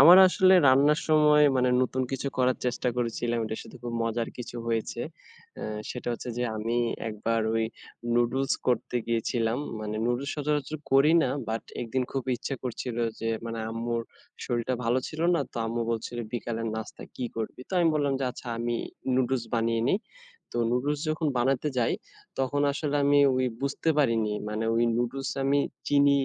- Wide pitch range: No, average, 3.2 semitones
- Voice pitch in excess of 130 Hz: No, low, 125 Hz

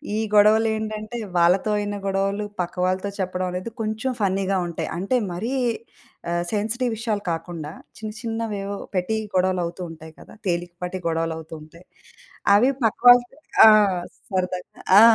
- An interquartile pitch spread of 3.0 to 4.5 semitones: Yes, average, 3.5 semitones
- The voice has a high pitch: Yes, high, 195 Hz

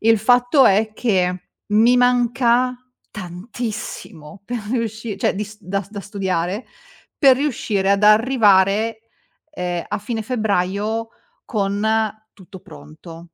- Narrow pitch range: No, average, 3.6 semitones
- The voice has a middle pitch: No, high, 210 Hz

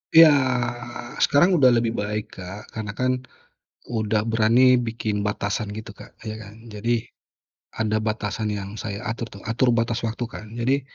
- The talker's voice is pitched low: Yes, low, 110 Hz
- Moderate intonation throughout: No, narrow, 2.0 semitones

